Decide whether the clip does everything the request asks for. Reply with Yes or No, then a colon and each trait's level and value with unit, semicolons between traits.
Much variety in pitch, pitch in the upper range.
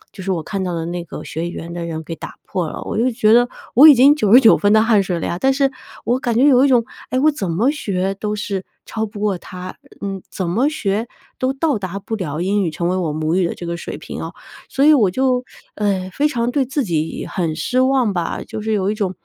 Yes: wide, 5.7 semitones; high, 205 Hz